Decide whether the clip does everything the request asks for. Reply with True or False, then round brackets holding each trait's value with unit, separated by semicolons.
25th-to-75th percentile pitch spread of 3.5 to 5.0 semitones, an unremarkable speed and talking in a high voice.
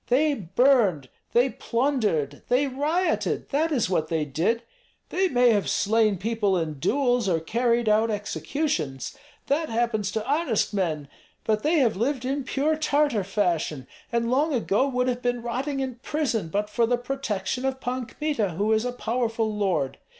True (4.7 semitones; 165 wpm; 235 Hz)